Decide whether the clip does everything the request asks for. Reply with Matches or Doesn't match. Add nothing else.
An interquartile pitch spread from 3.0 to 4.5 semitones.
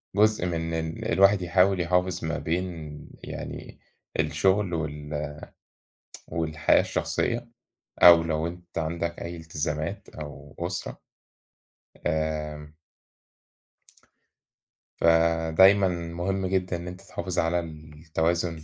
Doesn't match